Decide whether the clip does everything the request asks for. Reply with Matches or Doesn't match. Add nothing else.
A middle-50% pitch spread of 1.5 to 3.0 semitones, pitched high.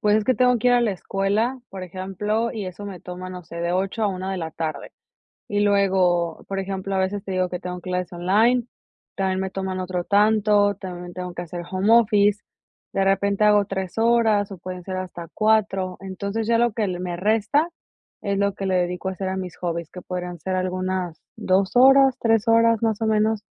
Matches